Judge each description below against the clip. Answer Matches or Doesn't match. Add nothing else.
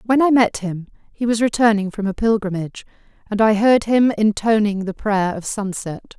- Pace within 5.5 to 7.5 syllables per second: Doesn't match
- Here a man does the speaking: Doesn't match